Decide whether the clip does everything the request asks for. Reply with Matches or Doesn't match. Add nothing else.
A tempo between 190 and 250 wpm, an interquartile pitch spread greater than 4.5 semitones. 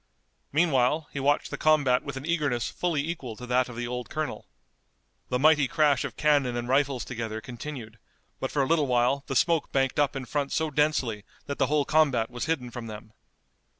Doesn't match